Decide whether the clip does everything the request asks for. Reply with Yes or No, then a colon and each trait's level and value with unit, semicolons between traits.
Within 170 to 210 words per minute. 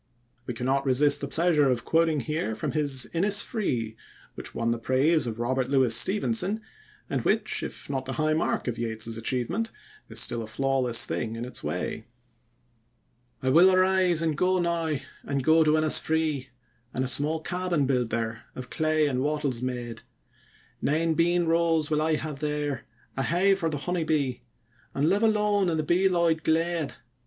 Yes: average, 175 wpm